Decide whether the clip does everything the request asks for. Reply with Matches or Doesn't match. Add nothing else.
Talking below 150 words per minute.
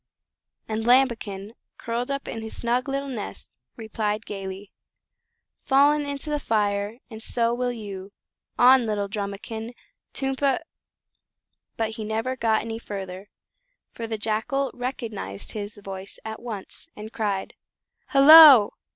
Matches